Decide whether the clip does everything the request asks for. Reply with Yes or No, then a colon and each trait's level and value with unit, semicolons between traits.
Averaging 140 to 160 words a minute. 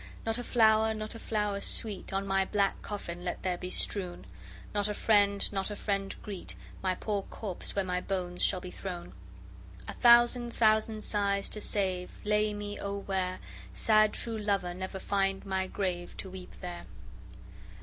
No: average, 170 wpm